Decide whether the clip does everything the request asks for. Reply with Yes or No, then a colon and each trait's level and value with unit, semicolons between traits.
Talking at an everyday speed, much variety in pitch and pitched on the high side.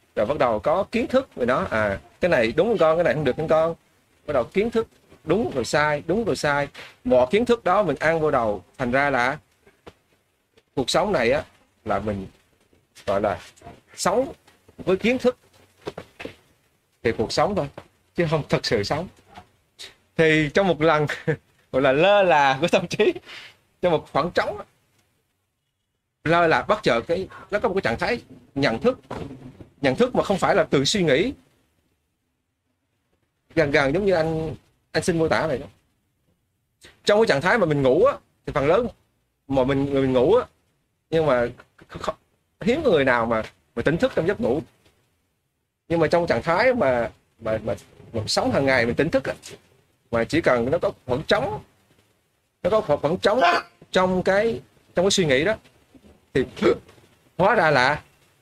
No: average, 185 wpm; wide, 6.4 semitones; medium, 150 Hz